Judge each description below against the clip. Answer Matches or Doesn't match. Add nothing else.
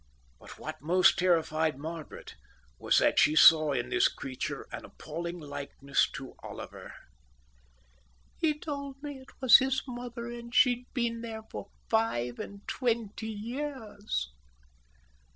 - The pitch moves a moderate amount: Doesn't match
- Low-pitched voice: Doesn't match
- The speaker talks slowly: Matches